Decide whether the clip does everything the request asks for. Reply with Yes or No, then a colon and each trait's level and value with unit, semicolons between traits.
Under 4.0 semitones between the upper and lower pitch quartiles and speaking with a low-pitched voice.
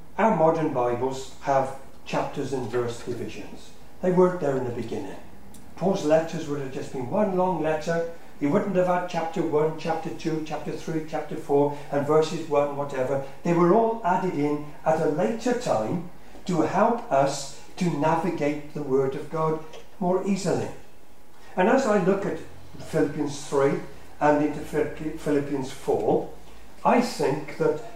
No: average, 3.1 semitones; medium, 155 Hz